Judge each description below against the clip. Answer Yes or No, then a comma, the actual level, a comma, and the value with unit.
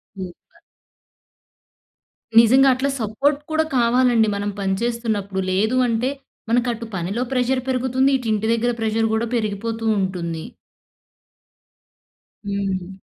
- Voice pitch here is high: Yes, high, 225 Hz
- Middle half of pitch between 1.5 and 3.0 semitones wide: No, average, 3.7 semitones